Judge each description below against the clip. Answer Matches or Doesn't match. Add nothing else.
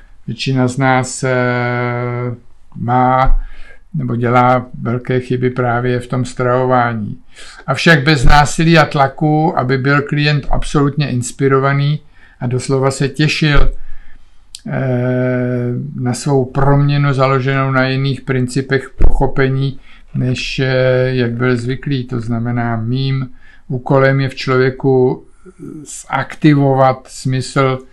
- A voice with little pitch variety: Matches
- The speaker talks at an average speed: Doesn't match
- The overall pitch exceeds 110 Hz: Matches